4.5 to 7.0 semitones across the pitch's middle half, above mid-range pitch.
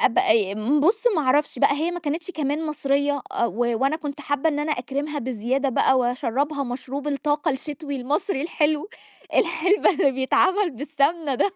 No: average, 2.8 semitones; very high, 285 Hz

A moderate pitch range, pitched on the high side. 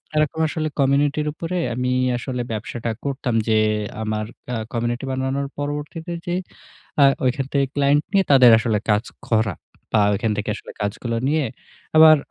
No: average, 4.3 semitones; low, 135 Hz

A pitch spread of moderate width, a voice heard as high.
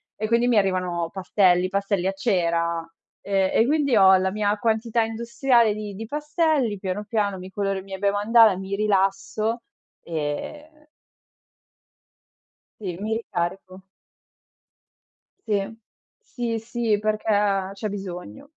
Yes: average, 3.1 semitones; high, 205 Hz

